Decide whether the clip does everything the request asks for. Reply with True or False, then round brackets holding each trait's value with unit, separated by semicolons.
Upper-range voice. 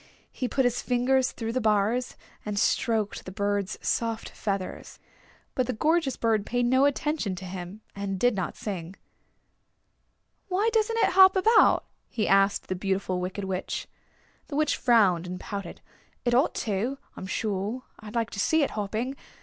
True (220 Hz)